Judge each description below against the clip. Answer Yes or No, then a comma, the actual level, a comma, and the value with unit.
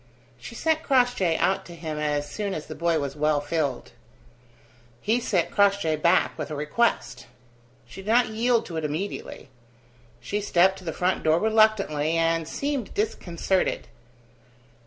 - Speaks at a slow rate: No, average, 155 wpm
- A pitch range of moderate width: No, wide, 5.7 semitones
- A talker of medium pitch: Yes, medium, 175 Hz